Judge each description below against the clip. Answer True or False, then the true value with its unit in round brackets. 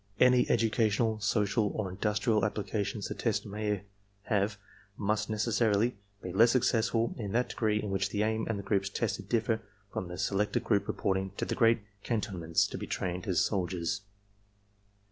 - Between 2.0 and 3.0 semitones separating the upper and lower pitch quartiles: True (2.4 semitones)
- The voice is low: True (105 Hz)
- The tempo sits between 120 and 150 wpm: False (165 wpm)